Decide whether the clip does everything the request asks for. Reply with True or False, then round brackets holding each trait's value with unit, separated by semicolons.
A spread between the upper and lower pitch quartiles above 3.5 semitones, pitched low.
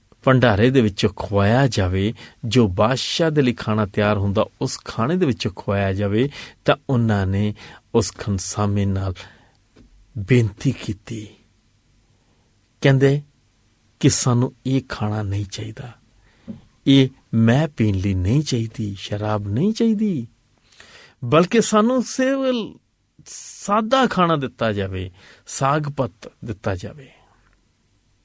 True (4.3 semitones; 115 Hz)